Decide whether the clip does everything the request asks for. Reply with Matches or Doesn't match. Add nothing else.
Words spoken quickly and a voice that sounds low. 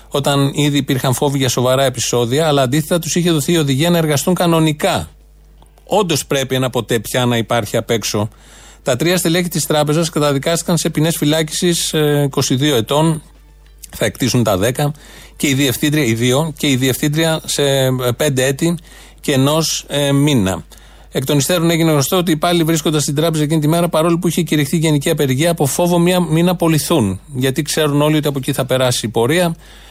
Doesn't match